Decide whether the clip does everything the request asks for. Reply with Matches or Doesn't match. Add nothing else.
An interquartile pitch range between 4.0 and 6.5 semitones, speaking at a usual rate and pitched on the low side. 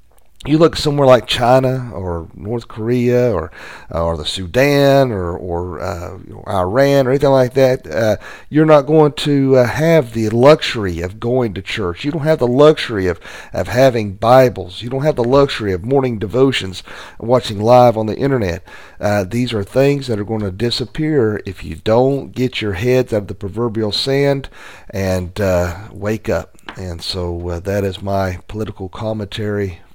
Matches